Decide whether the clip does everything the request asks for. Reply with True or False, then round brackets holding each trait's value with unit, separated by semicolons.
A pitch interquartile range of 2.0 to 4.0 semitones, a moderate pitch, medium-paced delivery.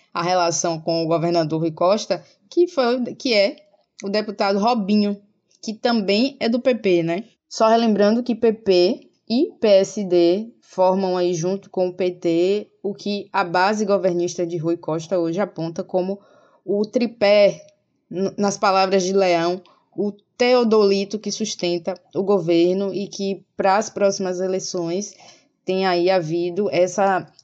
False (2.6 semitones; 195 Hz; 140 wpm)